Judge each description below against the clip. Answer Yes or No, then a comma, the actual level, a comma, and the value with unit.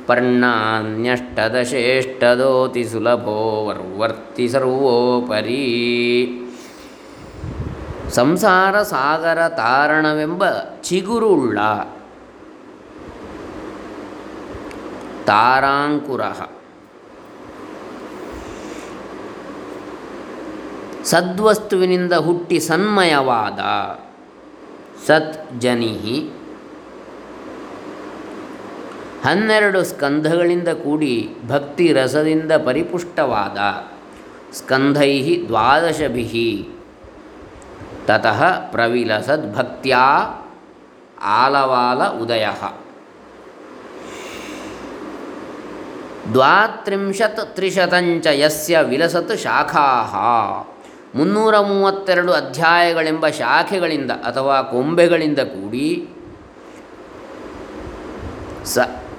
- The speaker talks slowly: Yes, slow, 35 wpm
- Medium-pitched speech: Yes, medium, 155 Hz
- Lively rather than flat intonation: Yes, wide, 6.3 semitones